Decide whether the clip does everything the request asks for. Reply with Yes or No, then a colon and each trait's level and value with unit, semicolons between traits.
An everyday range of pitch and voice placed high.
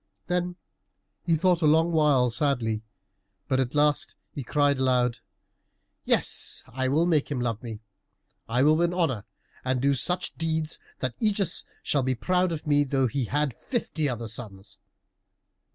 No: average, 4.5 semitones; medium, 140 Hz